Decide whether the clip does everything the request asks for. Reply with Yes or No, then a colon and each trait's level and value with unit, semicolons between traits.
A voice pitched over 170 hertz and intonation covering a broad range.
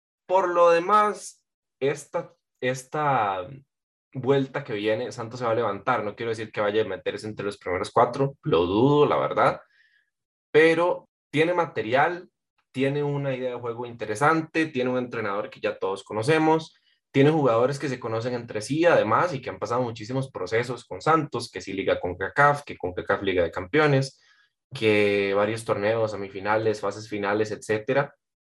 No: low, 135 Hz; wide, 5.9 semitones